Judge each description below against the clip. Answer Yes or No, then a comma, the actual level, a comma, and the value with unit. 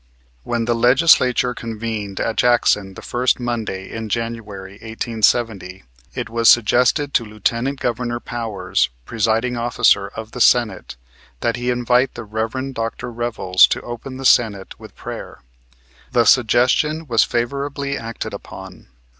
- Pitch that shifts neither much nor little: No, narrow, 2.0 semitones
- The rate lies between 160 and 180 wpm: No, slow, 135 wpm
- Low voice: Yes, low, 115 Hz